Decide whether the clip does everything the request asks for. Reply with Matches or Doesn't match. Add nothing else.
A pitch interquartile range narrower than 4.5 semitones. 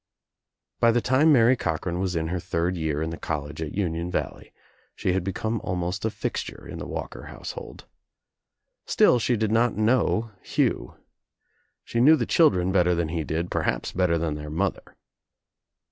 Doesn't match